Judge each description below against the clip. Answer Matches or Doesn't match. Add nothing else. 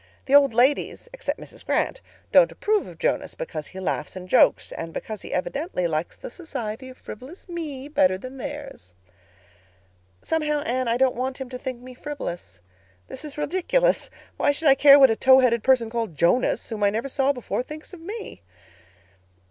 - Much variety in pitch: Doesn't match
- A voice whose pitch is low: Doesn't match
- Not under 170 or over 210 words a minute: Matches